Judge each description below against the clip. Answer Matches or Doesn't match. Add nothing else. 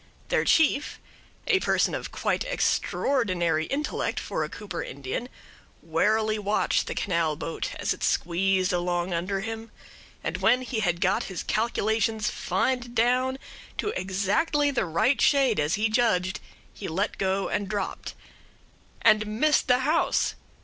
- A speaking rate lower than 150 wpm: Matches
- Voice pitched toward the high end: Matches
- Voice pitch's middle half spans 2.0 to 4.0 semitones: Doesn't match